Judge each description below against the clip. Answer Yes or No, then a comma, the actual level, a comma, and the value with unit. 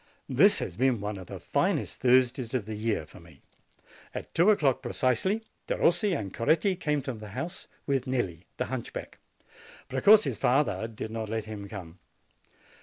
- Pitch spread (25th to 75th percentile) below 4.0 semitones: No, average, 4.6 semitones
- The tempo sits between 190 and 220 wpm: No, average, 165 wpm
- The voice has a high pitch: No, low, 120 Hz